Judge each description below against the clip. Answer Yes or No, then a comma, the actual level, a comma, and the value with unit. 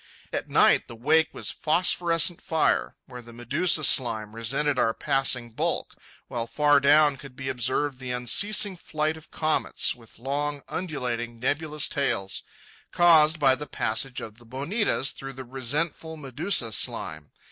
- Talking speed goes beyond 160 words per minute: No, average, 145 wpm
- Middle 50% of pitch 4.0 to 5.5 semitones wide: Yes, average, 4.4 semitones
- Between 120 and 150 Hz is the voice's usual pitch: Yes, medium, 140 Hz